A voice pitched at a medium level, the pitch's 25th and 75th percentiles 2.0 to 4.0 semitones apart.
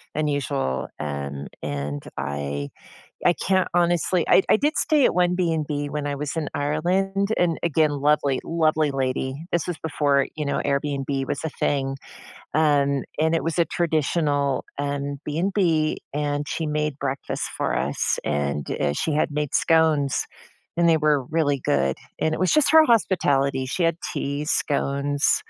Yes: medium, 150 Hz; average, 2.9 semitones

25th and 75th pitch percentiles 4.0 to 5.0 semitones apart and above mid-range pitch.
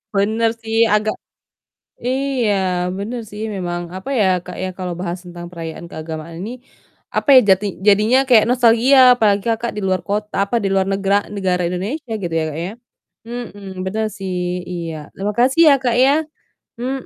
Yes: average, 4.3 semitones; high, 205 Hz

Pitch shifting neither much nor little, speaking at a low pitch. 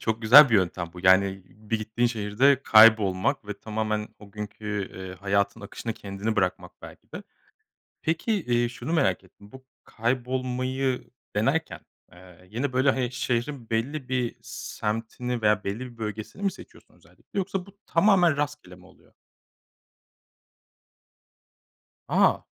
Yes: average, 4.2 semitones; low, 115 Hz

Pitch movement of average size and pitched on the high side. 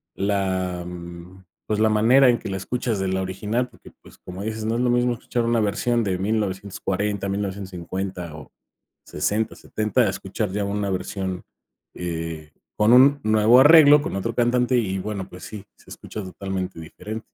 No: average, 3.5 semitones; low, 100 Hz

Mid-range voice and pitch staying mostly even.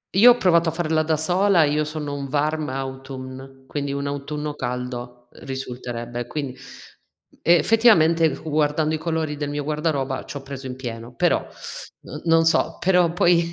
No: medium, 150 Hz; average, 3.4 semitones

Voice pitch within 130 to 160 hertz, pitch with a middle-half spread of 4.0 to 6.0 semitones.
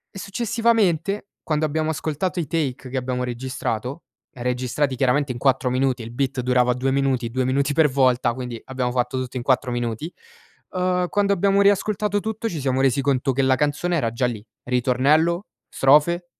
Yes: low, 135 Hz; average, 5.1 semitones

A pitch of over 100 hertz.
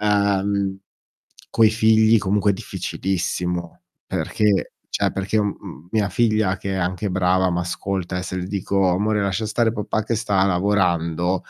No: very low, 95 Hz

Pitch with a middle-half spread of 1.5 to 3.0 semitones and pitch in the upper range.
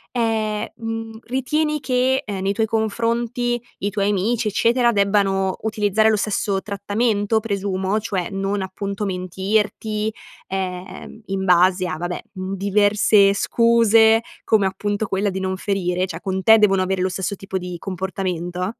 Yes: narrow, 2.6 semitones; high, 200 Hz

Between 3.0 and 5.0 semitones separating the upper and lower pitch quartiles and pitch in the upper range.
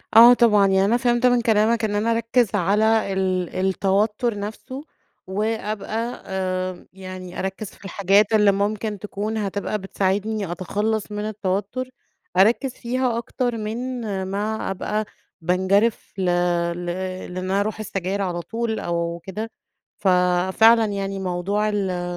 No: narrow, 2.6 semitones; high, 205 Hz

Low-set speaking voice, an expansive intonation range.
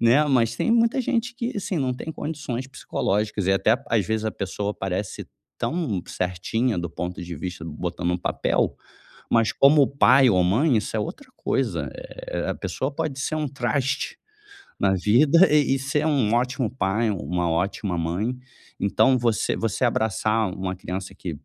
Yes: low, 115 Hz; wide, 6.6 semitones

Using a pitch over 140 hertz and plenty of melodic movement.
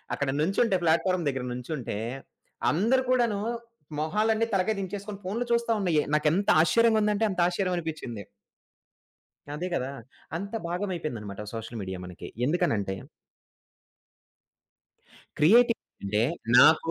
Yes: medium, 175 Hz; wide, 6.6 semitones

